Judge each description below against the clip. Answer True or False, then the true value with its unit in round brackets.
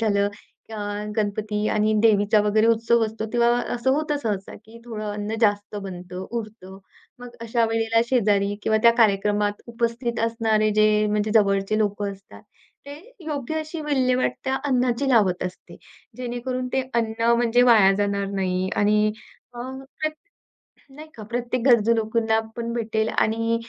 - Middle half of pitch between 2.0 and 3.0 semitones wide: True (2.6 semitones)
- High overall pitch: True (225 Hz)